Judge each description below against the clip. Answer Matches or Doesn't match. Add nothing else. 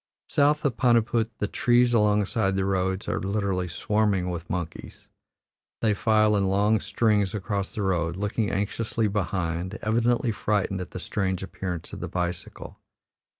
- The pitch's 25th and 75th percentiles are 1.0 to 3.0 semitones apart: Matches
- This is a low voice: Matches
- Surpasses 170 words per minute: Doesn't match